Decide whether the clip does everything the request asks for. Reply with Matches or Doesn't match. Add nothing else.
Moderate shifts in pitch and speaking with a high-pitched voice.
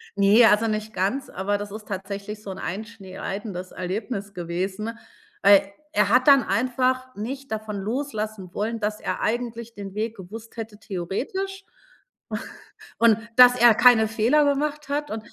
Matches